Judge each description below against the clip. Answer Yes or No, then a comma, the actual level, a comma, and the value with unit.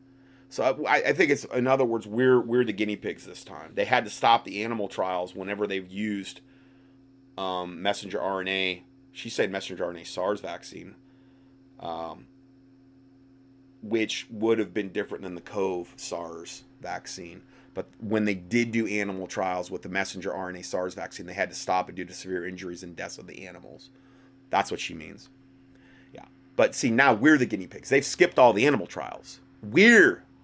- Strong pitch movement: Yes, wide, 5.9 semitones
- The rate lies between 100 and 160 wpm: No, average, 180 wpm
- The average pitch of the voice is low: Yes, low, 110 Hz